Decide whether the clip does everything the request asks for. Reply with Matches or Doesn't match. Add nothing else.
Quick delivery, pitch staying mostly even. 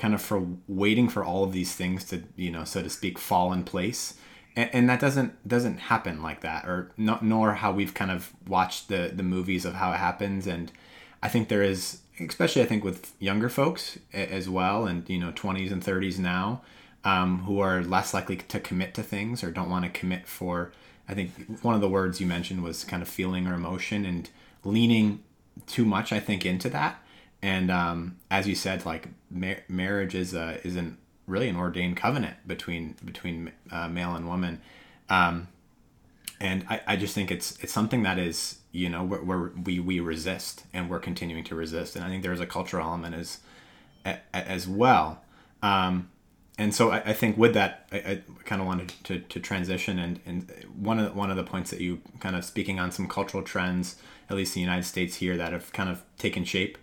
Matches